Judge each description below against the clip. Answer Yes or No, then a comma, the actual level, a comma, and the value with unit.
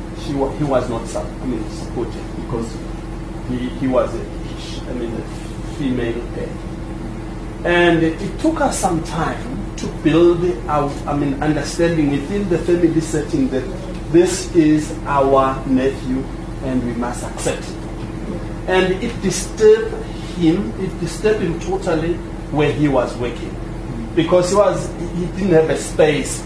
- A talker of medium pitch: Yes, medium, 160 Hz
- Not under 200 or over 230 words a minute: No, slow, 135 wpm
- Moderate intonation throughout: Yes, average, 4.3 semitones